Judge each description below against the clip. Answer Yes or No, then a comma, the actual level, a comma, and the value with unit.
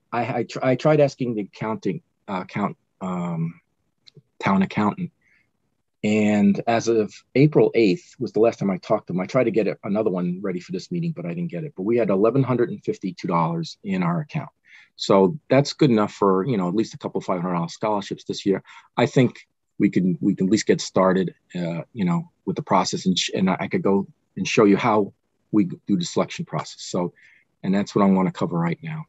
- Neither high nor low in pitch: No, low, 115 Hz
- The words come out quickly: Yes, fast, 215 wpm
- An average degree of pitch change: No, wide, 8.3 semitones